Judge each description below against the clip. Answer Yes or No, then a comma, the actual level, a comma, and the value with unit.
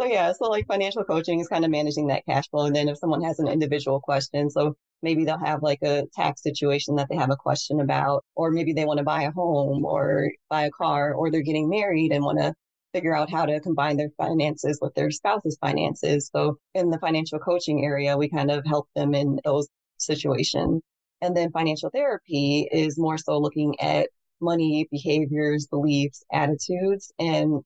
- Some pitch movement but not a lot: No, narrow, 2.0 semitones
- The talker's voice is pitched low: No, medium, 150 Hz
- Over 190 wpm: Yes, average, 200 wpm